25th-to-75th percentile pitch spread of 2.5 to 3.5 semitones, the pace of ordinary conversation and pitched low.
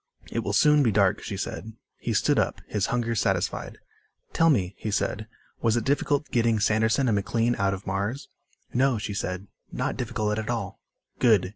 Yes: average, 3.1 semitones; average, 180 wpm; low, 110 Hz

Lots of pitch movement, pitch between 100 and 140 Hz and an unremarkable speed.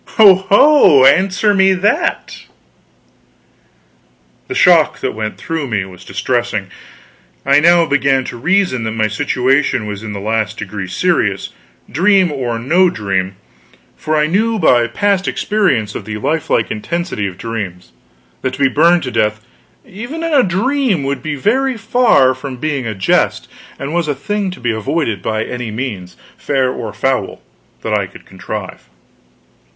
Yes: wide, 8.9 semitones; low, 135 Hz; average, 155 wpm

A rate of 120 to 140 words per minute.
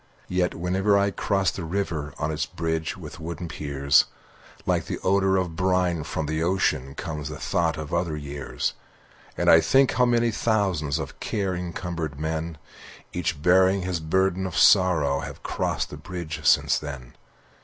No: average, 165 wpm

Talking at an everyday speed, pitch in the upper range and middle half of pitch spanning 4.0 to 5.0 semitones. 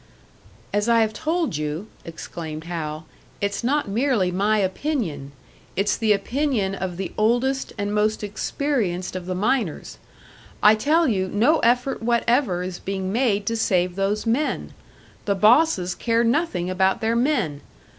Yes: average, 145 wpm; high, 210 Hz; average, 4.7 semitones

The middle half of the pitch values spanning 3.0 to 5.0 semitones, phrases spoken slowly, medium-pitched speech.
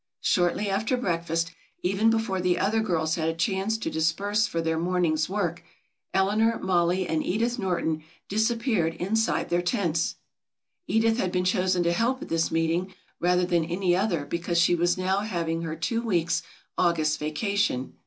No: average, 3.7 semitones; average, 165 wpm; medium, 180 Hz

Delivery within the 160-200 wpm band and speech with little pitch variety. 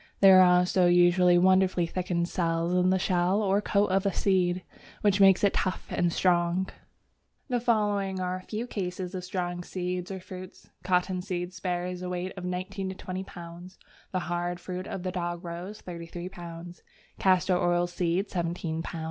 Yes: average, 175 wpm; narrow, 1.2 semitones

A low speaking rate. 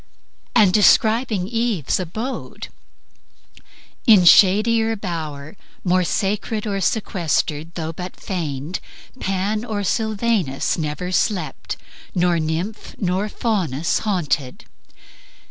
Yes: slow, 95 wpm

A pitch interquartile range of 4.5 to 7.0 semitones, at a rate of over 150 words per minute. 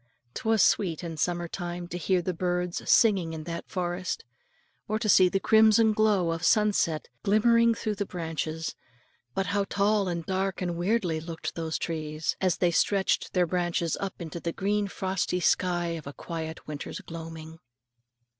No: average, 3.2 semitones; average, 165 wpm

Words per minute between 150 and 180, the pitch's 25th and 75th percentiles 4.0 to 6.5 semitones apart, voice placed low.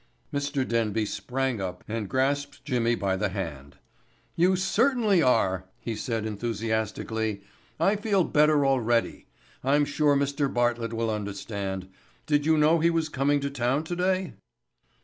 No: average, 140 wpm; wide, 5.4 semitones; low, 130 Hz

